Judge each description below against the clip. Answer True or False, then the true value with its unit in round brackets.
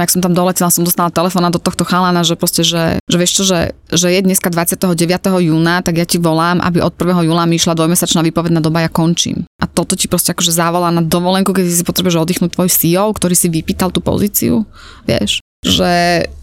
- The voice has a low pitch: False (175 Hz)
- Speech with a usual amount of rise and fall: False (1.3 semitones)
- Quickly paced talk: True (210 wpm)